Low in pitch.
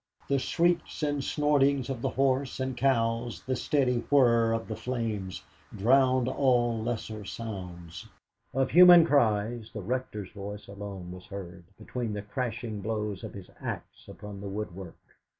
Yes: low, 115 Hz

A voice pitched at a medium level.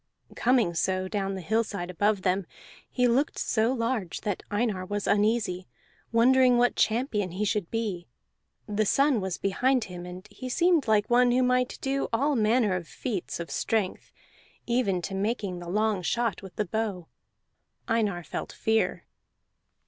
No: high, 215 Hz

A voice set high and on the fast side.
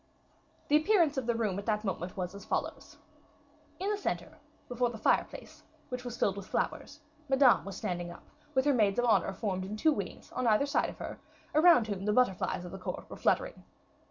Yes: high, 225 Hz; fast, 210 wpm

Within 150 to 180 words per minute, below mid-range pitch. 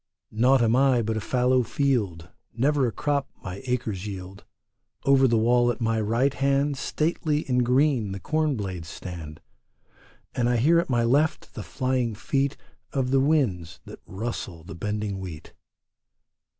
Yes: average, 160 wpm; low, 120 Hz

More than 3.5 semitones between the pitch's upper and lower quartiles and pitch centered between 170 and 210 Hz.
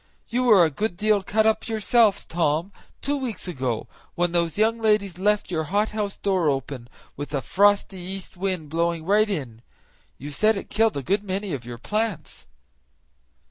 Yes: average, 5.1 semitones; high, 190 Hz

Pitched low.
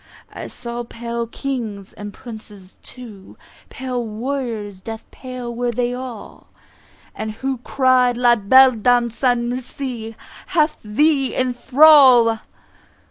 No: high, 245 Hz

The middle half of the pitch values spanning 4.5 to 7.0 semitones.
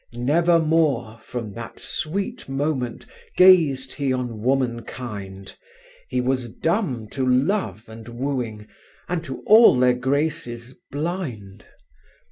Yes: average, 5.1 semitones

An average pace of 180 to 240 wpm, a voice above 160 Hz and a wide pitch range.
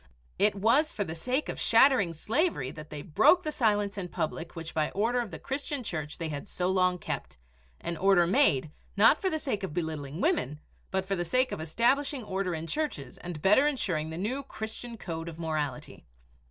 Yes: average, 200 wpm; high, 190 Hz; wide, 7.2 semitones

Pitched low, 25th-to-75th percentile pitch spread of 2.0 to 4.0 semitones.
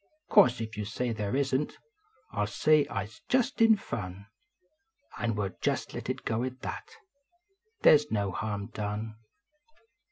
No: low, 110 Hz; average, 4.6 semitones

